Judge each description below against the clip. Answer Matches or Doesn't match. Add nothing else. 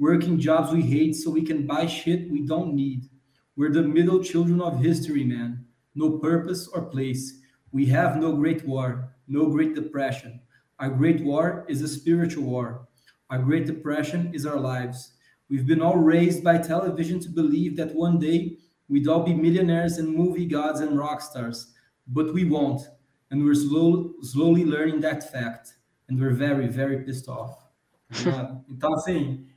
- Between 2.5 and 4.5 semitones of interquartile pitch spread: Matches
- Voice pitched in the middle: Matches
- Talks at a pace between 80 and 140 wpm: Doesn't match